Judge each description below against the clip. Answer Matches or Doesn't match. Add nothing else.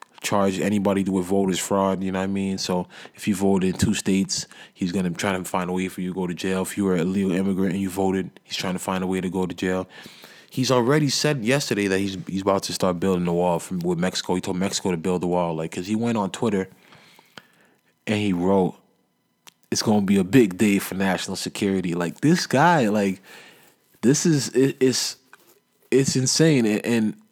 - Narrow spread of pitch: Matches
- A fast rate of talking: Matches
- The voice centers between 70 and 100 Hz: Matches